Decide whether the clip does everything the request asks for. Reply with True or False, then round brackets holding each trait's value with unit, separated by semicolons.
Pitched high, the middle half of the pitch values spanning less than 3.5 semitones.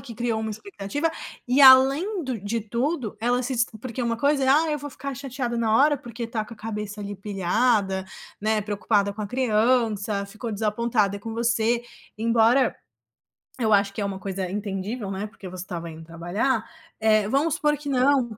False (225 Hz; 4.0 semitones)